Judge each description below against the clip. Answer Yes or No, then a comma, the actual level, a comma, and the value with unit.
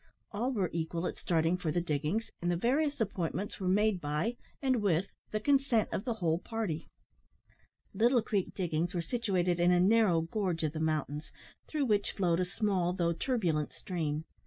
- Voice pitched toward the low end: No, medium, 180 Hz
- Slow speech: No, average, 180 wpm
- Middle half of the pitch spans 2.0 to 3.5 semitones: No, average, 4.8 semitones